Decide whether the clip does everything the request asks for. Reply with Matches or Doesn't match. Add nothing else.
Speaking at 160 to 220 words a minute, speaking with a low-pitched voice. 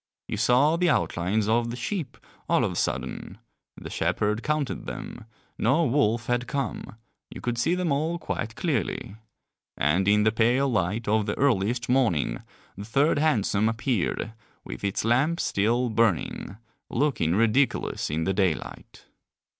Doesn't match